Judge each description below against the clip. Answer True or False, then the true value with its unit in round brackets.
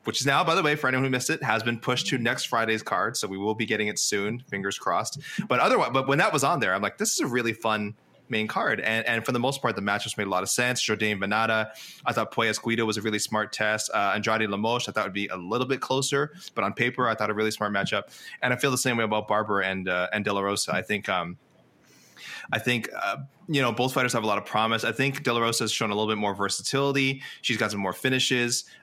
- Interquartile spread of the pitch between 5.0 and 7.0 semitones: False (3.4 semitones)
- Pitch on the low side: True (115 Hz)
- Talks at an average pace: False (280 wpm)